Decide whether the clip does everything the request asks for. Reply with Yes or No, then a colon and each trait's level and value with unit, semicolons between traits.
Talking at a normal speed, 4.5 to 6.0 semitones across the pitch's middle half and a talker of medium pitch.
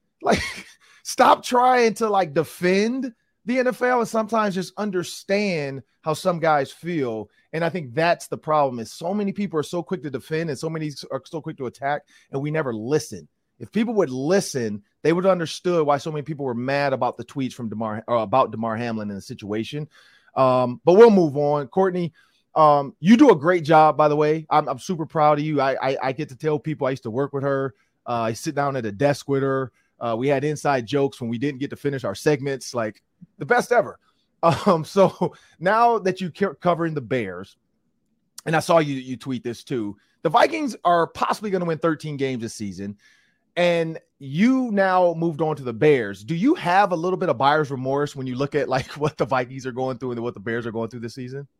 No: fast, 225 wpm; average, 5.1 semitones; medium, 150 Hz